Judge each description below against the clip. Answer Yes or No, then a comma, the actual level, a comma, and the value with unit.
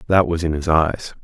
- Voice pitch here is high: No, very low, 80 Hz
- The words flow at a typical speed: No, fast, 245 wpm